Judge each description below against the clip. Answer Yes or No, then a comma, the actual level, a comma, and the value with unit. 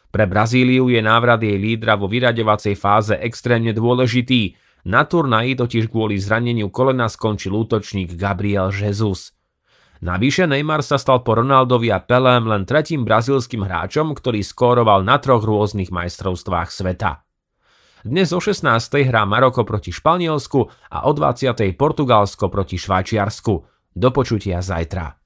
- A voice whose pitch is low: Yes, low, 110 Hz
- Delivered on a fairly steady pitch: No, average, 4.2 semitones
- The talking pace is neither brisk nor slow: Yes, average, 135 wpm